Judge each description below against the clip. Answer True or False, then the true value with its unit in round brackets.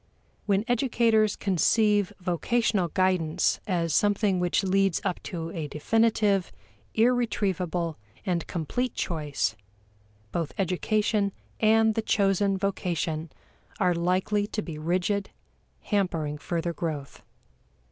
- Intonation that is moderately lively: True (3.8 semitones)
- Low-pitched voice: False (190 Hz)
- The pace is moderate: False (105 wpm)